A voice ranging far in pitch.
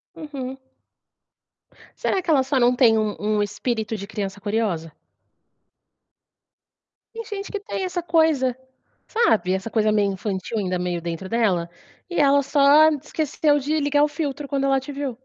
Yes: wide, 6.2 semitones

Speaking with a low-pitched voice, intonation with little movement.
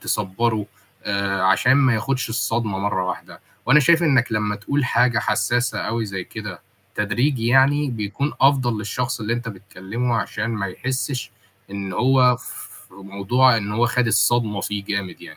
No: low, 115 Hz; average, 3.8 semitones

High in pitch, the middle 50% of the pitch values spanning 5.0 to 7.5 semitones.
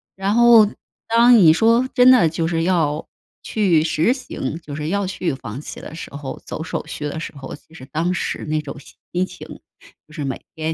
No: medium, 165 Hz; wide, 5.4 semitones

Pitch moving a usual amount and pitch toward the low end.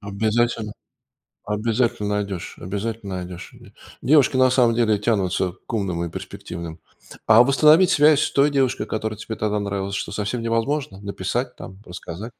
Yes: average, 3.5 semitones; low, 110 Hz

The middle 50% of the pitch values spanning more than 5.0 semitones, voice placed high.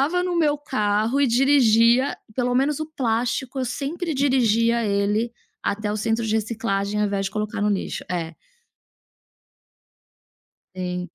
No: average, 4.6 semitones; high, 230 Hz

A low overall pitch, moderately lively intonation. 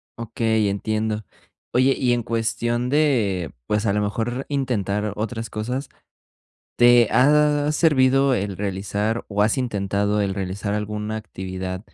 Yes: low, 110 Hz; average, 3.4 semitones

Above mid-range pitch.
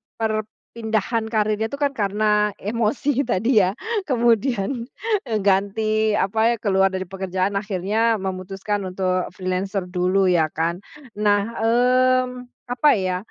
Yes: high, 210 Hz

